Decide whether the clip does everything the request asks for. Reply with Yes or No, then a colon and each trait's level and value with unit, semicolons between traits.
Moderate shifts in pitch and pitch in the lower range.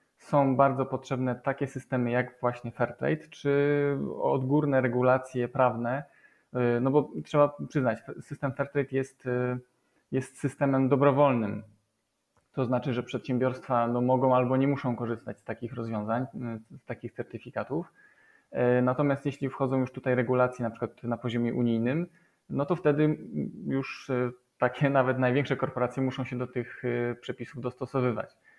No: narrow, 2.2 semitones; low, 130 Hz